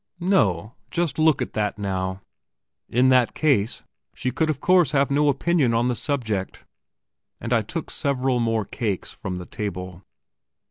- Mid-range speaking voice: No, low, 120 Hz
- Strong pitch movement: Yes, wide, 5.9 semitones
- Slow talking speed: No, average, 155 wpm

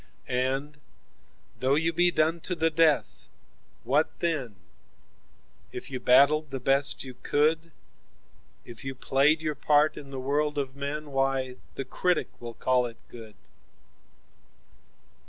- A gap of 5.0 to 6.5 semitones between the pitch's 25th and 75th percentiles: No, average, 3.0 semitones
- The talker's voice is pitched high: No, medium, 140 Hz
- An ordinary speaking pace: No, slow, 130 wpm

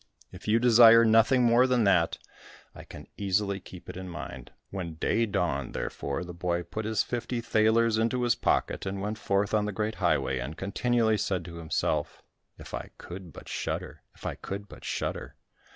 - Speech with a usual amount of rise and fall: Yes, average, 4.4 semitones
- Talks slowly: No, average, 185 wpm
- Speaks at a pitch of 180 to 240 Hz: No, low, 105 Hz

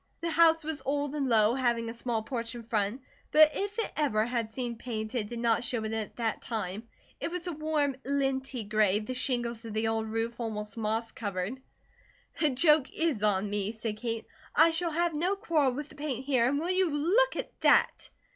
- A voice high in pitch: Yes, high, 245 Hz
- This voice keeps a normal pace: No, fast, 210 wpm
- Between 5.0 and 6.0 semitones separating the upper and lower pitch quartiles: Yes, average, 5.3 semitones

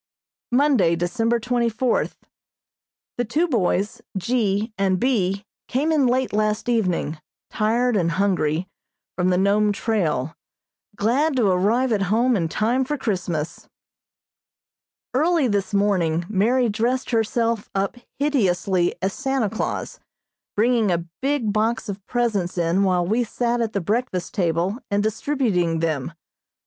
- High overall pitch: Yes, high, 210 Hz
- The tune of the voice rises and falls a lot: No, average, 4.8 semitones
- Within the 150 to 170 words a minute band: No, slow, 135 wpm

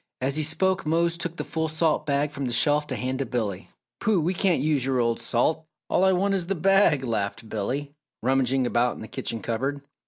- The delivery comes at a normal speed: No, fast, 220 wpm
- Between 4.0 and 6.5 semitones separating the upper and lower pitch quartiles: Yes, average, 5.0 semitones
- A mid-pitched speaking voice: Yes, medium, 145 Hz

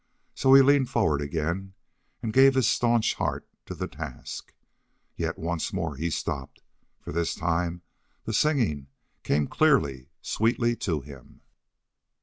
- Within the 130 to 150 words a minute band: Yes, slow, 135 wpm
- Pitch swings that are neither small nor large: No, wide, 7.9 semitones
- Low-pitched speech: Yes, very low, 85 Hz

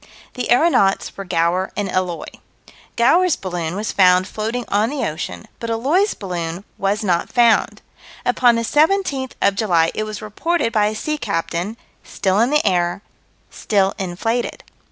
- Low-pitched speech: No, high, 210 Hz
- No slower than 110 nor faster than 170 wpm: Yes, average, 155 wpm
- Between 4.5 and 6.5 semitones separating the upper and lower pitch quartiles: Yes, average, 4.8 semitones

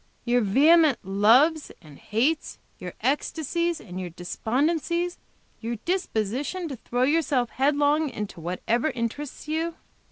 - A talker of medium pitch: No, very high, 270 Hz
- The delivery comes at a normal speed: No, slow, 120 wpm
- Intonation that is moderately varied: No, wide, 6.3 semitones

